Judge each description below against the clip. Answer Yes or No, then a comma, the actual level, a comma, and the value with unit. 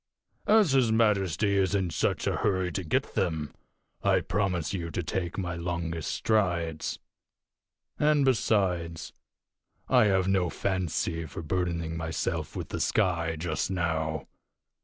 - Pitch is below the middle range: Yes, very low, 90 Hz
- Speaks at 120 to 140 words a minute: Yes, slow, 135 wpm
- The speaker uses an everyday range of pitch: Yes, average, 3.2 semitones